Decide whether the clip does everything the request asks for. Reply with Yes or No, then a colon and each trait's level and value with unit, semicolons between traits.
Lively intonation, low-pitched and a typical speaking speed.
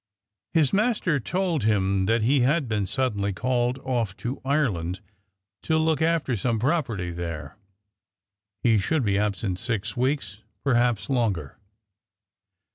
No: wide, 5.9 semitones; low, 120 Hz; slow, 125 wpm